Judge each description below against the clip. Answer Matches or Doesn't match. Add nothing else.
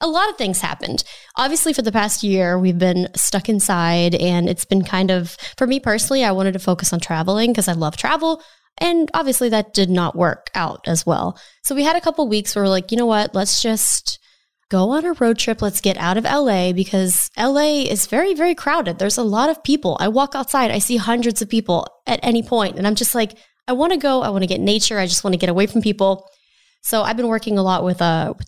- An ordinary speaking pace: Doesn't match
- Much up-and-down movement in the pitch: Matches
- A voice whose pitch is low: Doesn't match